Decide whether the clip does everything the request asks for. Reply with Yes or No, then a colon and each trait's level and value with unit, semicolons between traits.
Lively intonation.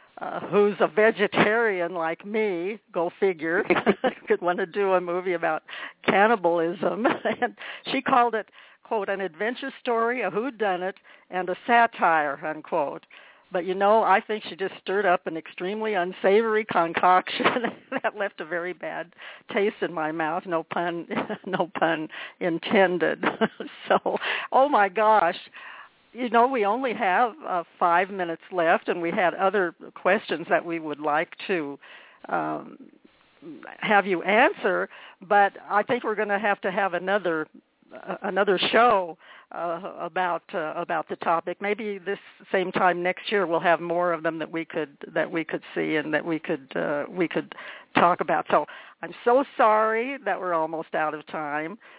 No: average, 4.2 semitones